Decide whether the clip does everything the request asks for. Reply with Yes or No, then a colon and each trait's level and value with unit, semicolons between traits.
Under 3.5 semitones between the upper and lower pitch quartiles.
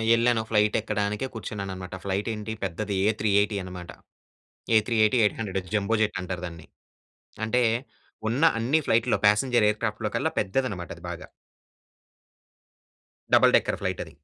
Yes: narrow, 2.6 semitones